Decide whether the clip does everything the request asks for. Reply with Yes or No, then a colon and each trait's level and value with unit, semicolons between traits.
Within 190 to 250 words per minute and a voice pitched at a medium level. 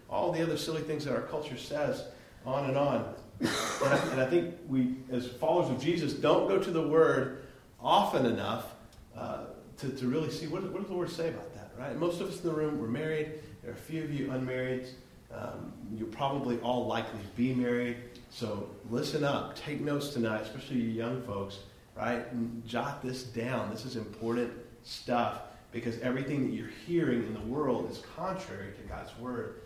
No: average, 200 wpm; low, 130 Hz